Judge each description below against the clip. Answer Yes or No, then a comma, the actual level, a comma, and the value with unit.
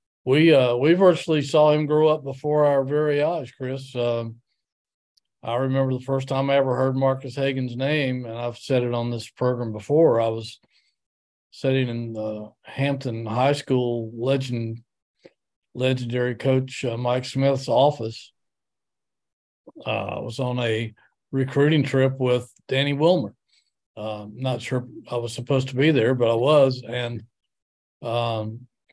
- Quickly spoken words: No, average, 150 wpm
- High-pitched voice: No, low, 130 Hz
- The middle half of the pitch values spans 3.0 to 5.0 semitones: No, narrow, 2.5 semitones